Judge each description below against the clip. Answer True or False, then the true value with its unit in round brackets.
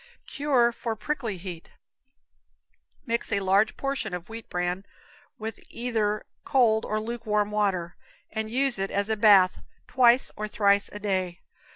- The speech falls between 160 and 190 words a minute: False (145 wpm)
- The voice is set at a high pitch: True (215 Hz)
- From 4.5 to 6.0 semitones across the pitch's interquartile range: False (3.1 semitones)